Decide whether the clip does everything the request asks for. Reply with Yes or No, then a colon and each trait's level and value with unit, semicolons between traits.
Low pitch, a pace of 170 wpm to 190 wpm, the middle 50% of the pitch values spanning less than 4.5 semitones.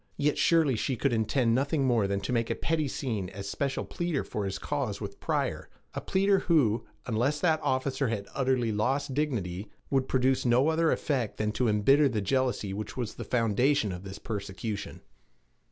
No: low, 125 Hz; average, 185 wpm; average, 4.9 semitones